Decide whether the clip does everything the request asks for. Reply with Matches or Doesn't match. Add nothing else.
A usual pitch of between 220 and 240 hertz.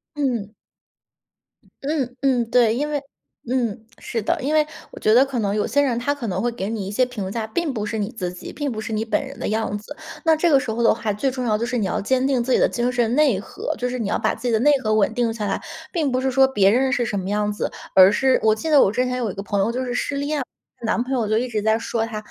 Matches